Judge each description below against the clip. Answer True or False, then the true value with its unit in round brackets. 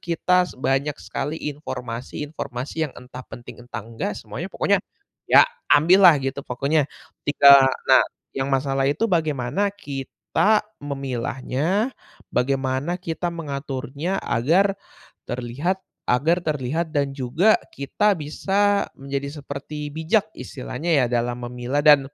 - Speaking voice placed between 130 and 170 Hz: True (140 Hz)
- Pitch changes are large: False (3.9 semitones)